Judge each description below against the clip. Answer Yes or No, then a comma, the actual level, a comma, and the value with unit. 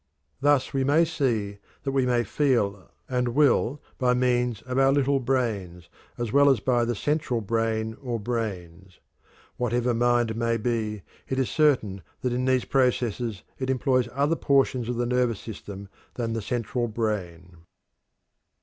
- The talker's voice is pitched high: No, low, 120 Hz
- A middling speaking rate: Yes, average, 155 wpm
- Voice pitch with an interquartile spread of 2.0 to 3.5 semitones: Yes, average, 3.0 semitones